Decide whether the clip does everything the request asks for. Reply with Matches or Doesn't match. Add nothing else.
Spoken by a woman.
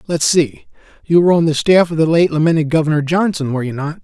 Doesn't match